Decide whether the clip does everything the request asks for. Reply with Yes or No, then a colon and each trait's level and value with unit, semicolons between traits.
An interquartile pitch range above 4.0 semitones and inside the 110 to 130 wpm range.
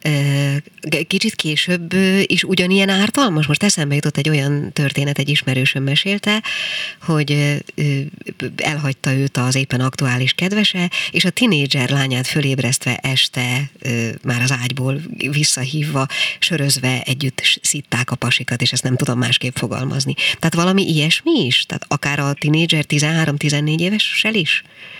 Yes: average, 4.5 semitones; average, 125 wpm